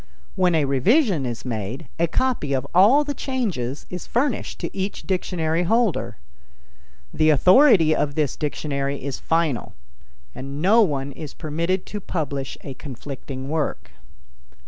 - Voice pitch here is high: No, medium, 155 Hz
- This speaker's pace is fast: No, average, 140 wpm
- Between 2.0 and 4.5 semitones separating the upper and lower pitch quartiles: No, wide, 5.5 semitones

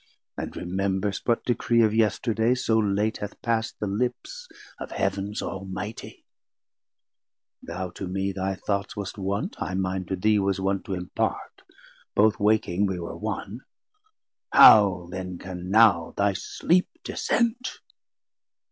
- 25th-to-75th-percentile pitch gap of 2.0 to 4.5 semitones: Yes, average, 2.7 semitones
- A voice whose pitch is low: Yes, low, 100 Hz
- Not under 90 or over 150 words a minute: Yes, slow, 135 wpm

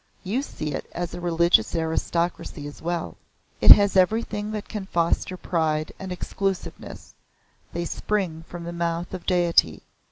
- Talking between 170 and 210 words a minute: No, average, 150 wpm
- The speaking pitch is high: No, medium, 175 Hz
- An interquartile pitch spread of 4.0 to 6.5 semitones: No, narrow, 2.4 semitones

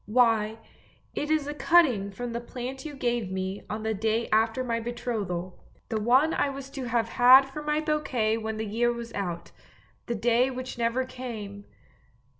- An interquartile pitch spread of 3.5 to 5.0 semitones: No, average, 3.1 semitones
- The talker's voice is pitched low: No, high, 235 Hz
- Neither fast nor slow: Yes, average, 190 wpm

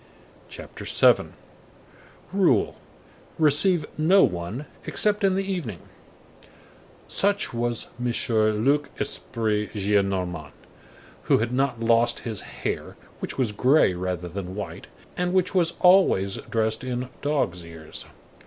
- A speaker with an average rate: No, slow, 105 wpm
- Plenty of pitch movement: Yes, wide, 8.1 semitones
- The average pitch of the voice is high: No, low, 120 Hz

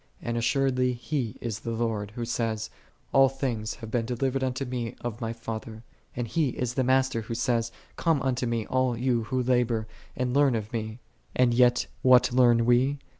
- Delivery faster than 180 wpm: Yes, average, 195 wpm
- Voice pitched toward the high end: No, low, 120 Hz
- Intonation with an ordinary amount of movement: No, narrow, 2.0 semitones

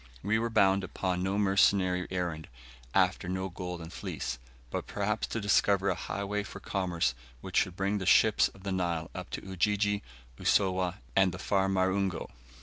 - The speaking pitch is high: No, very low, 95 Hz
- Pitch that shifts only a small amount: Yes, narrow, 1.8 semitones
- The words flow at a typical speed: Yes, average, 160 wpm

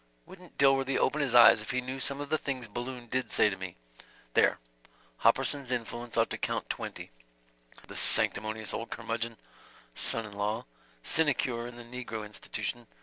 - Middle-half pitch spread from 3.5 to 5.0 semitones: No, average, 3.0 semitones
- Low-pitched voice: Yes, low, 120 Hz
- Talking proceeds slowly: No, average, 165 wpm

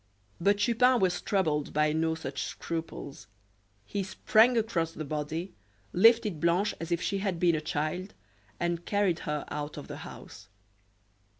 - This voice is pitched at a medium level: Yes, medium, 170 Hz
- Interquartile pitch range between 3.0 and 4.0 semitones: No, average, 4.4 semitones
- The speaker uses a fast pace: No, average, 155 wpm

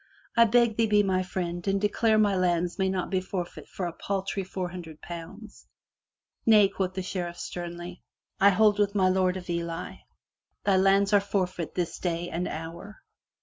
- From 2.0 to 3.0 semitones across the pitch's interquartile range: Yes, narrow, 2.4 semitones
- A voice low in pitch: No, medium, 185 Hz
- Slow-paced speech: No, average, 190 wpm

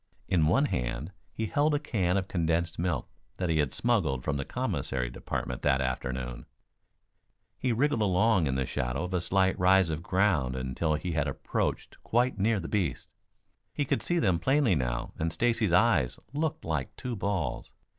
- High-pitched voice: No, very low, 90 Hz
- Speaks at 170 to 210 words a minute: Yes, average, 175 wpm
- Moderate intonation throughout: No, wide, 7.8 semitones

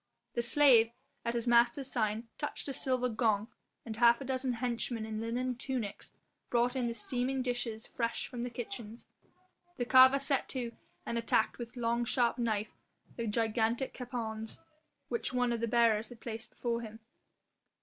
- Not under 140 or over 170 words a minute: Yes, average, 165 wpm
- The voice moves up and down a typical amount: No, narrow, 1.8 semitones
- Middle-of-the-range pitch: No, high, 235 Hz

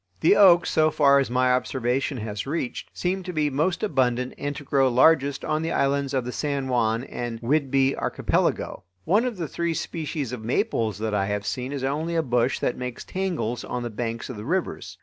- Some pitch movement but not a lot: Yes, average, 4.5 semitones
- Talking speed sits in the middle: No, fast, 210 wpm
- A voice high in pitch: No, low, 135 Hz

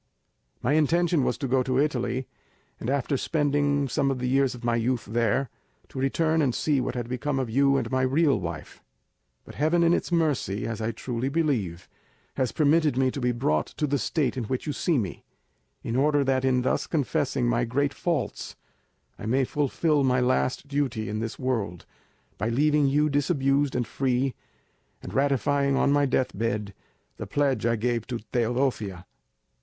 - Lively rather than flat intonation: No, average, 3.2 semitones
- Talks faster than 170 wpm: Yes, average, 180 wpm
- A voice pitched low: Yes, low, 130 Hz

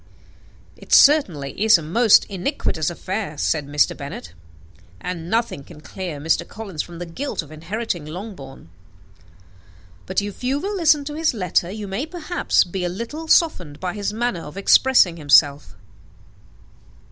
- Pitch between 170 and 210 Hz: Yes, high, 190 Hz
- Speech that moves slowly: No, average, 150 wpm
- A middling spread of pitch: No, wide, 7.1 semitones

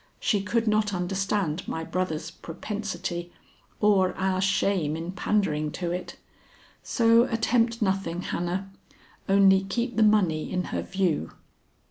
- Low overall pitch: No, high, 190 Hz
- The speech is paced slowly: Yes, slow, 125 wpm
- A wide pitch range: No, average, 3.2 semitones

